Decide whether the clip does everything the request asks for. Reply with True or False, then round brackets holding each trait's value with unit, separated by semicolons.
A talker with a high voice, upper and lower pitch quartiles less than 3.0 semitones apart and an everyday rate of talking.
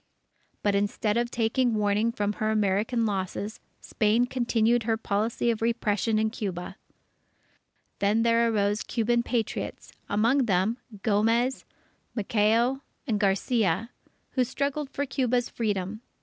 False (225 Hz; 2.5 semitones; 120 wpm)